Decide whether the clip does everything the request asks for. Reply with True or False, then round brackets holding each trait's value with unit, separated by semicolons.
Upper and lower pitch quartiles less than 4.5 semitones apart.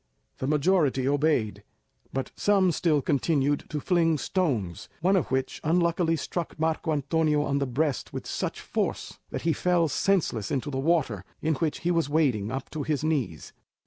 True (3.6 semitones)